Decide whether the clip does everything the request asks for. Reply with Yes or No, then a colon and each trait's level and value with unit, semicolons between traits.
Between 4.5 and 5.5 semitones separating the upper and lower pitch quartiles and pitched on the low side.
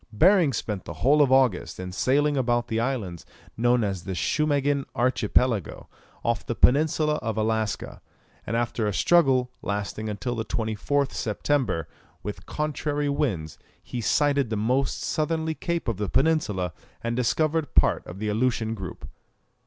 Yes: average, 5.2 semitones; low, 120 Hz